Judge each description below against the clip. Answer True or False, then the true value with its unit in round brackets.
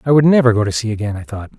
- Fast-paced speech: True (340 wpm)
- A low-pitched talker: True (120 Hz)